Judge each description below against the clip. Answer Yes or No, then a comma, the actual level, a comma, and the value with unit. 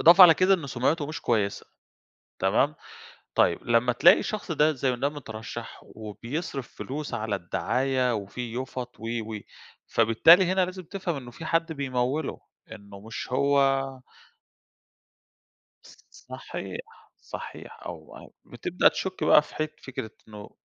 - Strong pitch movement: Yes, wide, 5.7 semitones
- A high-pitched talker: No, low, 135 Hz